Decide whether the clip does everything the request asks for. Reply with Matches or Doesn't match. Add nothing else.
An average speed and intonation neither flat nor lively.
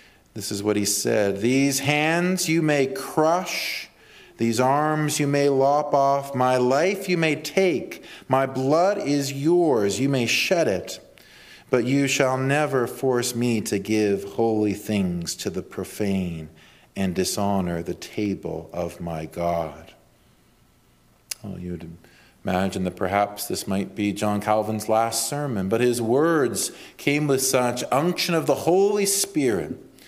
Doesn't match